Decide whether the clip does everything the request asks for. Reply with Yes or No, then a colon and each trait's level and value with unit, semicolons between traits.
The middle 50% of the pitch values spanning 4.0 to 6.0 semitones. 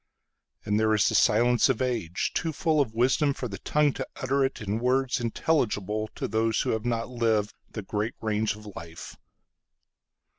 No: average, 3.3 semitones